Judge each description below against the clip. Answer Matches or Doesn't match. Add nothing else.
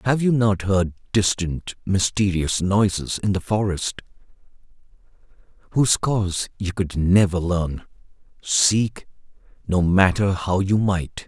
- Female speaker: Doesn't match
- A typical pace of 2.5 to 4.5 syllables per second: Matches